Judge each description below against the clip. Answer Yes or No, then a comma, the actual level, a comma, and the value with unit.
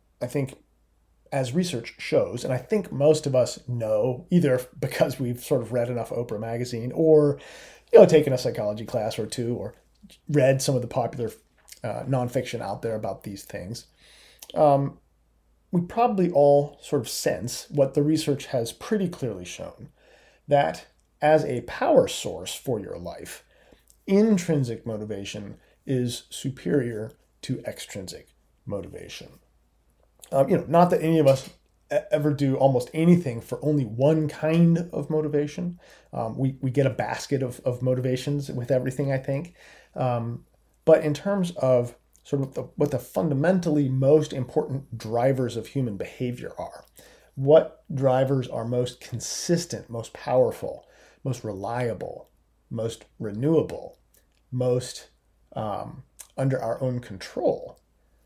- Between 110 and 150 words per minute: Yes, average, 140 wpm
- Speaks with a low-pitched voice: Yes, low, 130 Hz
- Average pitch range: Yes, average, 4.2 semitones